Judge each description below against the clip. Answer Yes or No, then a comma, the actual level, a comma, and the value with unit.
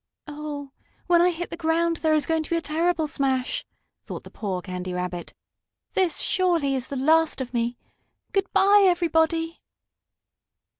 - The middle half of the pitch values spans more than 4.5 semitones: No, average, 4.1 semitones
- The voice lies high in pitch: Yes, very high, 320 Hz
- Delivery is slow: No, average, 160 wpm